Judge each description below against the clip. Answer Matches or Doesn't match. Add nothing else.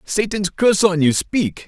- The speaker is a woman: Doesn't match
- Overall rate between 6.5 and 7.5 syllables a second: Doesn't match